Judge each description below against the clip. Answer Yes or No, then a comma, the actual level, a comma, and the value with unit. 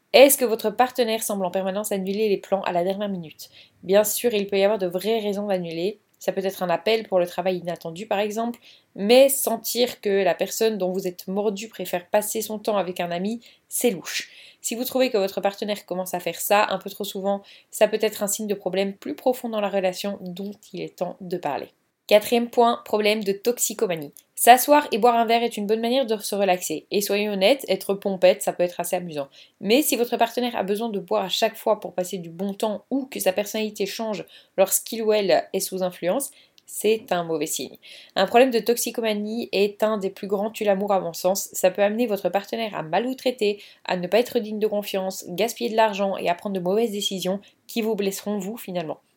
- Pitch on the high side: Yes, high, 205 Hz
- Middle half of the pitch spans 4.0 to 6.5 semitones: No, average, 2.9 semitones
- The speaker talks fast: Yes, fast, 225 wpm